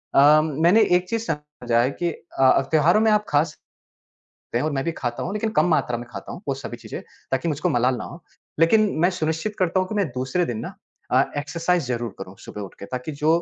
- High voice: No, medium, 155 Hz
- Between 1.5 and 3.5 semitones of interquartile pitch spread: No, wide, 5.6 semitones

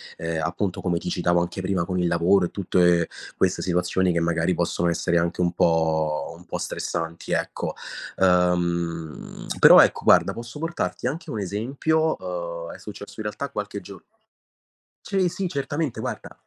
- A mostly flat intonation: No, average, 3.5 semitones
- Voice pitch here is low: Yes, very low, 90 Hz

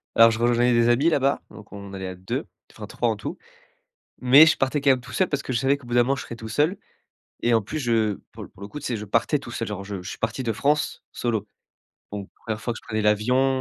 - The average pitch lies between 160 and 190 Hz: No, low, 120 Hz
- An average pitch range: Yes, average, 4.0 semitones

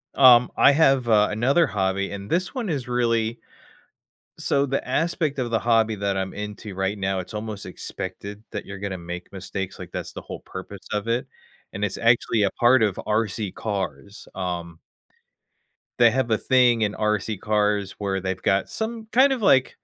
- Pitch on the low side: Yes, low, 105 Hz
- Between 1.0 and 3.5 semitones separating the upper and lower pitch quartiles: No, average, 4.0 semitones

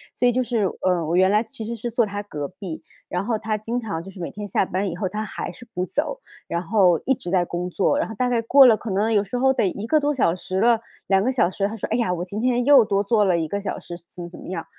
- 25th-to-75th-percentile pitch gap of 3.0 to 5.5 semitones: Yes, average, 4.4 semitones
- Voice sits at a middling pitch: No, high, 205 Hz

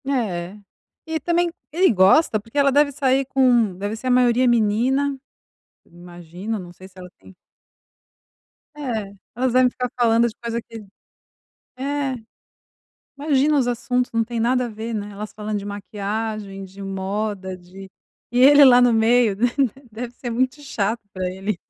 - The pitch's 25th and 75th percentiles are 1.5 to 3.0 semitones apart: No, average, 4.3 semitones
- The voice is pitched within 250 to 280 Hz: No, high, 230 Hz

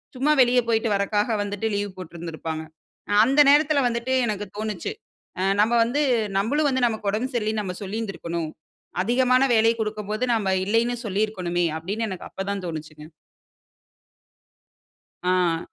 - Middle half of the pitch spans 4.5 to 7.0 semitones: No, average, 4.0 semitones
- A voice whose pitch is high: Yes, high, 210 Hz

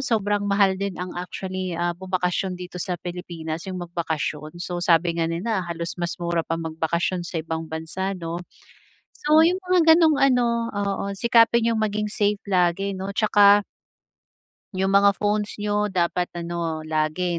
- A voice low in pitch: No, medium, 185 Hz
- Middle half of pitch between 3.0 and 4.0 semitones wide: Yes, average, 3.4 semitones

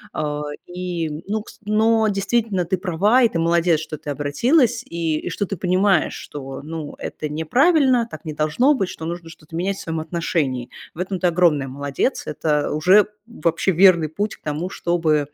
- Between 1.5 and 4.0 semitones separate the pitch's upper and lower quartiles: No, average, 4.7 semitones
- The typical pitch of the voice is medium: Yes, medium, 170 Hz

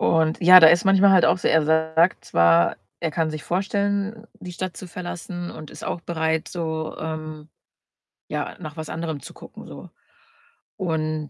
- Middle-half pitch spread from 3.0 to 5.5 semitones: No, narrow, 2.5 semitones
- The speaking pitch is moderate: Yes, medium, 160 Hz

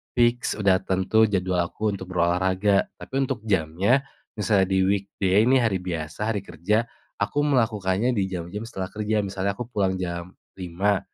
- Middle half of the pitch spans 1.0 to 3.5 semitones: Yes, average, 2.9 semitones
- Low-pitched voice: Yes, low, 100 Hz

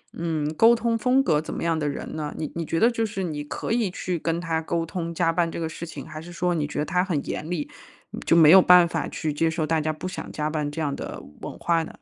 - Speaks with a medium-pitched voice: Yes, medium, 165 Hz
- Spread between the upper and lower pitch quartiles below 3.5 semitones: Yes, narrow, 2.5 semitones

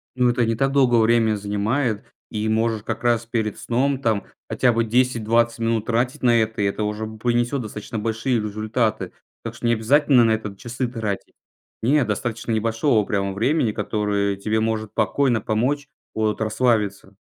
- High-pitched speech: No, low, 115 Hz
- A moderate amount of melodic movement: No, narrow, 2.0 semitones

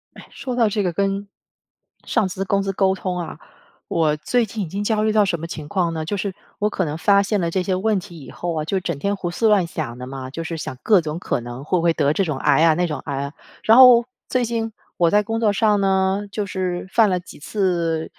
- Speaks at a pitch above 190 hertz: No, medium, 185 Hz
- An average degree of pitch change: Yes, average, 3.9 semitones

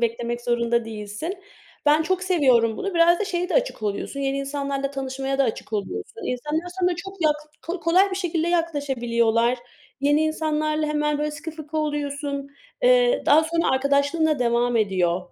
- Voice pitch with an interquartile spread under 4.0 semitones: No, wide, 5.4 semitones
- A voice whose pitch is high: Yes, very high, 290 Hz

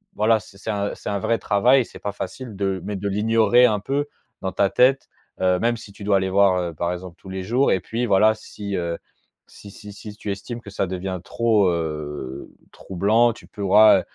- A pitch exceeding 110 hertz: No, low, 100 Hz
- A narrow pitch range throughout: No, average, 3.0 semitones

